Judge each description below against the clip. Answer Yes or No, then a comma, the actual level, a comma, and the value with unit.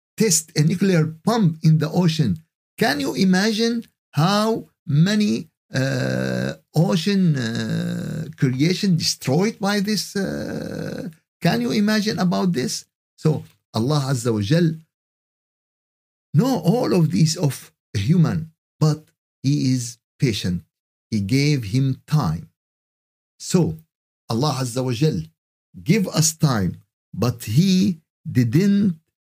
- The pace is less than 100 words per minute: No, average, 115 wpm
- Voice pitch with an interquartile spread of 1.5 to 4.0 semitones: No, average, 5.3 semitones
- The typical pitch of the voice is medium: Yes, medium, 160 Hz